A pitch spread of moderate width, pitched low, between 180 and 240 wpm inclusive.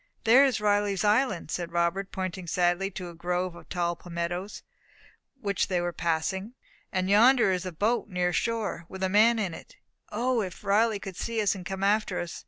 No: average, 3.2 semitones; high, 190 Hz; average, 190 wpm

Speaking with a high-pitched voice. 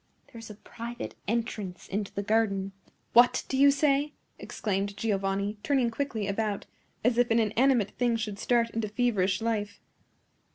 Yes: high, 225 Hz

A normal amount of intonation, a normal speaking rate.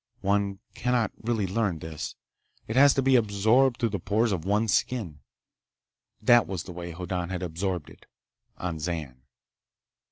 Yes: average, 4.8 semitones; average, 155 wpm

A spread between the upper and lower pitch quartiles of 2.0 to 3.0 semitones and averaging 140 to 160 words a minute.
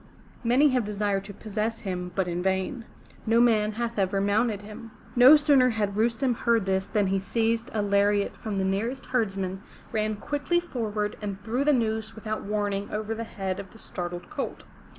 No: average, 2.7 semitones; average, 185 wpm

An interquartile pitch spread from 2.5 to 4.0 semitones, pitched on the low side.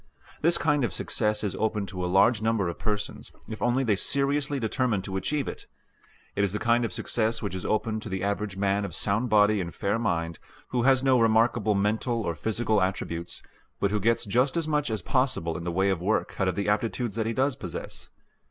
Yes: average, 3.5 semitones; low, 110 Hz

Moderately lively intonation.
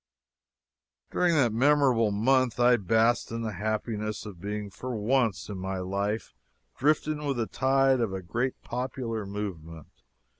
Yes: average, 4.1 semitones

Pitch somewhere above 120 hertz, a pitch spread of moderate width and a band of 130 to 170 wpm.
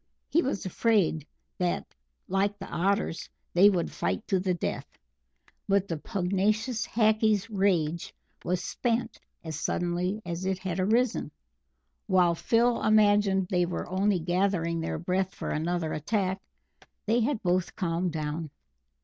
Yes: high, 190 Hz; average, 3.2 semitones; slow, 135 wpm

